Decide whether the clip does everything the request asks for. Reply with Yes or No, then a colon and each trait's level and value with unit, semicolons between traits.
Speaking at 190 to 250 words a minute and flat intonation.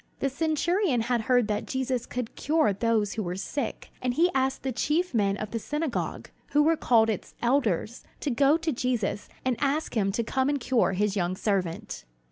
No: average, 195 wpm; average, 4.9 semitones